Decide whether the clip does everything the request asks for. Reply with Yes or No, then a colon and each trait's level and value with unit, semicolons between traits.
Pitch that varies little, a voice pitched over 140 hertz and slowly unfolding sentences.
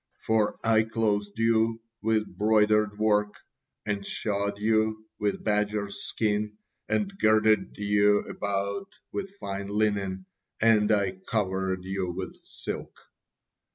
No: narrow, 1.4 semitones; low, 105 Hz; slow, 115 wpm